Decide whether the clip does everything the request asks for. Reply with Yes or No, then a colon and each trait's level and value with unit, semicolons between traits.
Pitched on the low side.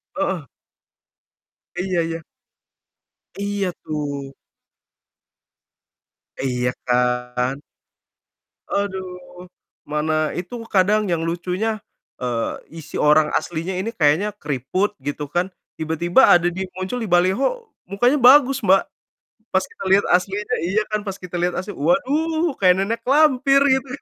No: medium, 185 Hz